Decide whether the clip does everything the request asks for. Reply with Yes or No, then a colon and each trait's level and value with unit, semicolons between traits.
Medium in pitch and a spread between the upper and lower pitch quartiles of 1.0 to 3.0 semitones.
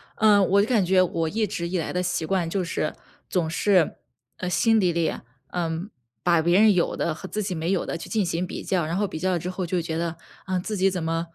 Yes: medium, 180 Hz; narrow, 2.6 semitones